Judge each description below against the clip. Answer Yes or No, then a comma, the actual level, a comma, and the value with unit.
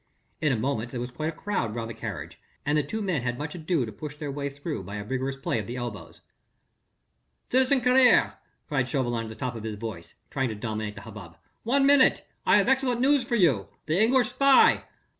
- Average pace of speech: No, fast, 220 wpm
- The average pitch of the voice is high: No, medium, 140 Hz